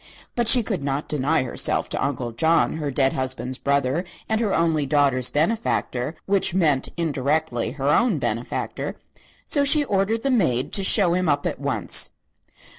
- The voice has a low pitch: No, medium, 150 Hz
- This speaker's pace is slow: No, average, 165 wpm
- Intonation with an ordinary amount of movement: No, wide, 6.3 semitones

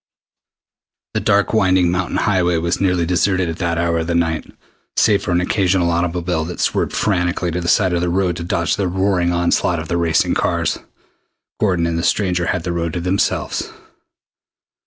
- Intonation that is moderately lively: No, narrow, 1.5 semitones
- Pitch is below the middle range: Yes, very low, 90 Hz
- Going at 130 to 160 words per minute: No, average, 185 wpm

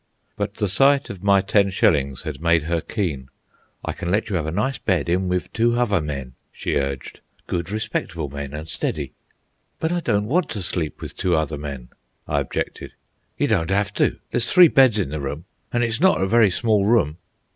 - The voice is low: Yes, very low, 90 Hz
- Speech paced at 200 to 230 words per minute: Yes, fast, 205 wpm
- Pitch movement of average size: No, wide, 6.4 semitones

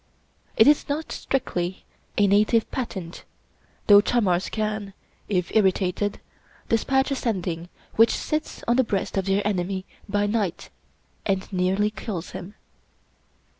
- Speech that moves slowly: Yes, slow, 130 wpm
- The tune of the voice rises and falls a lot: No, average, 3.2 semitones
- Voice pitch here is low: No, high, 205 Hz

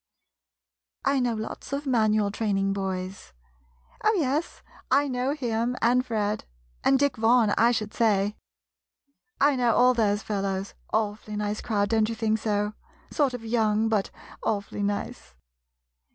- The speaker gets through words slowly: No, average, 150 wpm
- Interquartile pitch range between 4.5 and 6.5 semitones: No, average, 3.2 semitones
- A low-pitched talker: No, high, 220 Hz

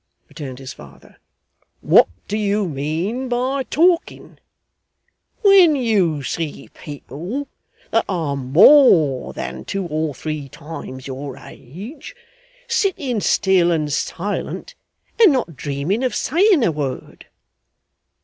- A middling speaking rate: No, slow, 110 wpm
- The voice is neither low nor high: Yes, medium, 170 Hz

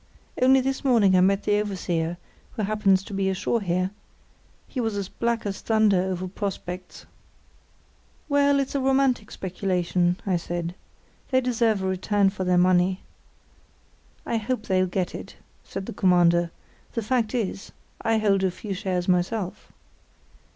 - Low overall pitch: No, high, 195 Hz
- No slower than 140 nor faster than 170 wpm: Yes, average, 150 wpm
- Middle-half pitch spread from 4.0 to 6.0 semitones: No, average, 3.5 semitones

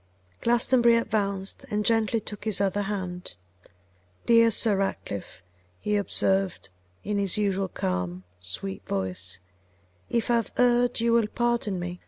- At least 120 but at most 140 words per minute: Yes, slow, 135 wpm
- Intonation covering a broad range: No, average, 4.5 semitones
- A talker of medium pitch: No, high, 205 Hz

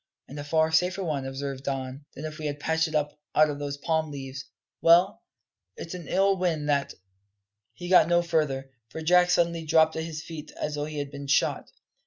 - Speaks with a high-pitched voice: No, medium, 155 Hz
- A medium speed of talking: No, fast, 215 wpm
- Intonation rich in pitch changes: No, average, 2.8 semitones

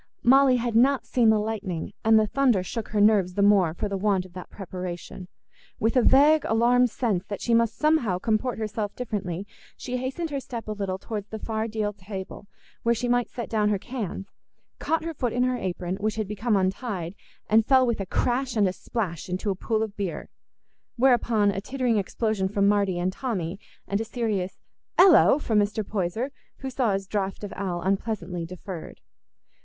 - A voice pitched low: No, high, 215 Hz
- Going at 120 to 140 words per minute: No, average, 190 wpm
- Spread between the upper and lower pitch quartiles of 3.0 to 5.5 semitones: Yes, average, 3.9 semitones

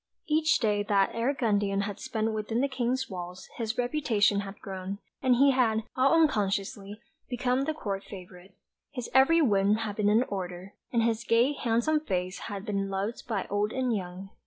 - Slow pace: No, average, 180 wpm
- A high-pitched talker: Yes, high, 215 Hz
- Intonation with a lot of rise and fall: No, average, 4.3 semitones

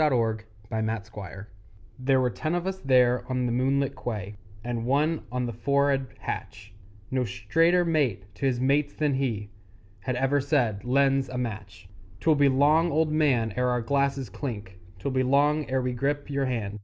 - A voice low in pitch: Yes, low, 130 Hz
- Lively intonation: No, average, 3.7 semitones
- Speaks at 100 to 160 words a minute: No, average, 180 wpm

